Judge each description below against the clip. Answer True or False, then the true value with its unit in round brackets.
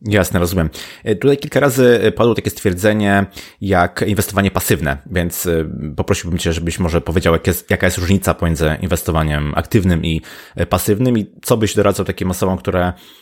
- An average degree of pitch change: True (3.7 semitones)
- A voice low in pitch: True (95 Hz)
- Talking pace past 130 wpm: True (155 wpm)